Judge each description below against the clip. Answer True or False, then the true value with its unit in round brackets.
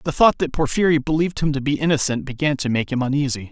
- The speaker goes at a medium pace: False (240 wpm)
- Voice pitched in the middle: True (145 Hz)